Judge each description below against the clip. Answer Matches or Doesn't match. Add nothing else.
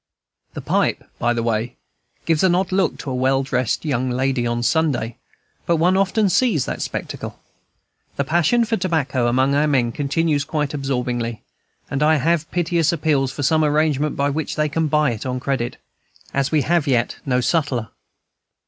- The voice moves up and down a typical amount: Matches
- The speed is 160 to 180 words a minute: Matches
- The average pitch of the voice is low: Doesn't match